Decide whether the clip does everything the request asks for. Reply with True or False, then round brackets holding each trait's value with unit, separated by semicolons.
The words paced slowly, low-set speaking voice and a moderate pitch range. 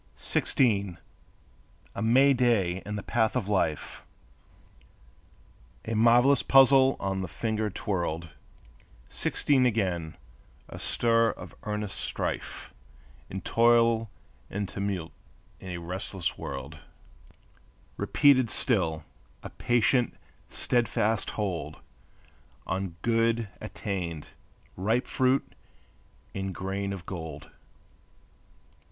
True (95 wpm; 105 Hz; 4.0 semitones)